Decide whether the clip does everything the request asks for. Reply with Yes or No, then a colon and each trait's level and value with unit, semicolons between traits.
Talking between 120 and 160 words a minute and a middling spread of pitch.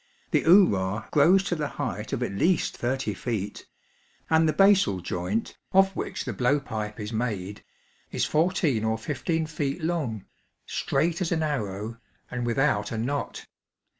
No: average, 155 wpm; wide, 6.9 semitones